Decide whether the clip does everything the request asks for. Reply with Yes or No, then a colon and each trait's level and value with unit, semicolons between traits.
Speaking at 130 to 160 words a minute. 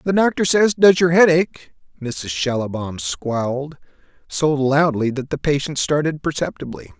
Yes: average, 145 wpm